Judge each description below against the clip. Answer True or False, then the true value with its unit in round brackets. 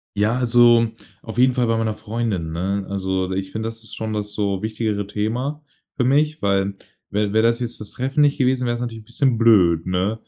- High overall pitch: False (110 Hz)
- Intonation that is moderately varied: True (3.2 semitones)